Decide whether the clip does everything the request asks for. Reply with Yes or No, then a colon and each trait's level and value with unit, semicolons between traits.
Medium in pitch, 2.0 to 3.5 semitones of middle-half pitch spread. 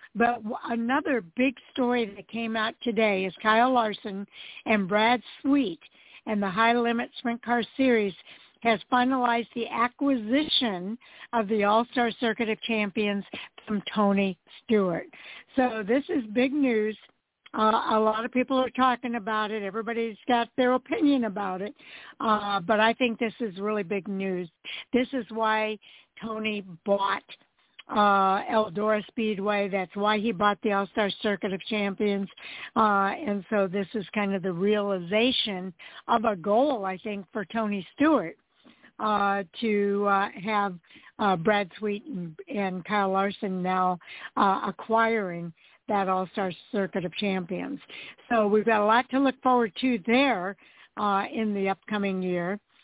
No: high, 215 Hz; average, 2.9 semitones